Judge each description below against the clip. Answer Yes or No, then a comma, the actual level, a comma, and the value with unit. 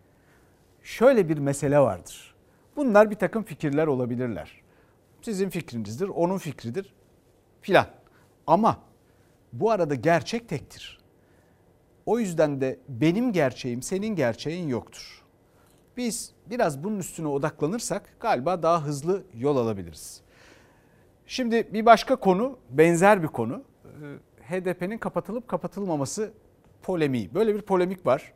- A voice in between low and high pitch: Yes, medium, 160 Hz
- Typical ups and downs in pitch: No, wide, 7.6 semitones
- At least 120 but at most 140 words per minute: No, average, 110 wpm